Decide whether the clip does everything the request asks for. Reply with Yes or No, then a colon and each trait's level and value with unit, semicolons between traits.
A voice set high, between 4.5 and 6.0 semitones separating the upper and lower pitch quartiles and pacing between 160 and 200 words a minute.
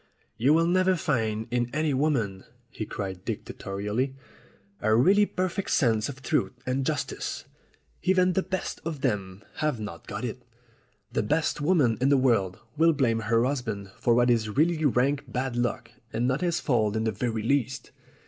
No: low, 125 Hz; wide, 5.6 semitones; average, 175 wpm